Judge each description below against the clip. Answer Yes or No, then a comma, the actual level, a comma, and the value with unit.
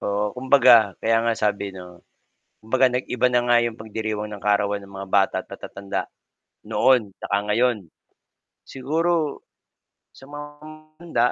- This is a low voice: Yes, low, 110 Hz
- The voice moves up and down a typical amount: Yes, average, 4.2 semitones